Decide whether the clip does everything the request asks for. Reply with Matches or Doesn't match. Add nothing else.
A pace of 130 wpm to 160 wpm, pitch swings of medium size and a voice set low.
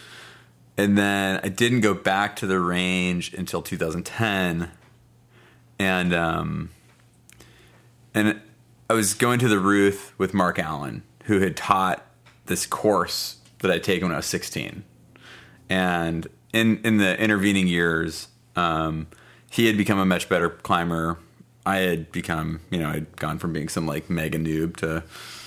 Matches